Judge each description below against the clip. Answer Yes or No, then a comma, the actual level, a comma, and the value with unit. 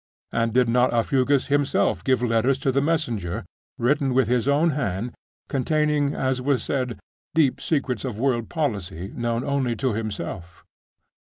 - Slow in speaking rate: No, average, 150 wpm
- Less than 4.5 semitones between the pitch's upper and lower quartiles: Yes, average, 3.4 semitones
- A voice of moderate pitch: No, low, 130 Hz